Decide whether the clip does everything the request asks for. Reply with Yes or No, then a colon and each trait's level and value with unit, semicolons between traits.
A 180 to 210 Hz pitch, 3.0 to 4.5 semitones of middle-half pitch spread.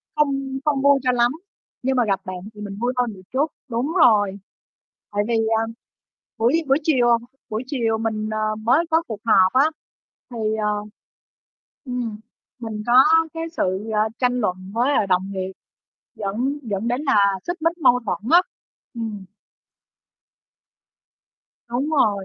No: high, 235 Hz; average, 4.1 semitones